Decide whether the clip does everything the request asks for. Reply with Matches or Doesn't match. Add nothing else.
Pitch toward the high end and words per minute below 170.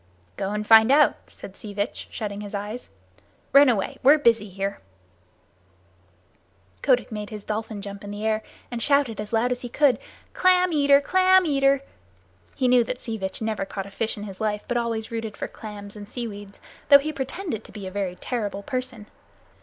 Doesn't match